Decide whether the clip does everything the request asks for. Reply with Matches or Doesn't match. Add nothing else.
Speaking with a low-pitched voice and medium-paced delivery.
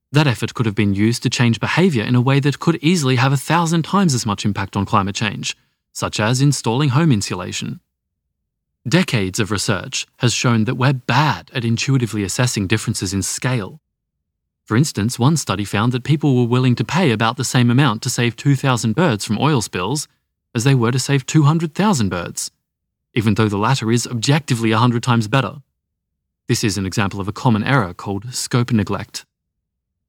Matches